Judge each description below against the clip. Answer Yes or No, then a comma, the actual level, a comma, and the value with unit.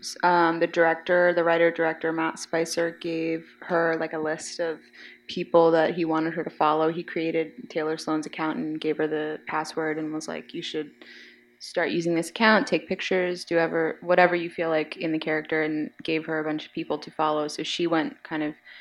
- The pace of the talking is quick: Yes, fast, 215 wpm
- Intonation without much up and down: Yes, narrow, 1.5 semitones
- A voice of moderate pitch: Yes, medium, 160 Hz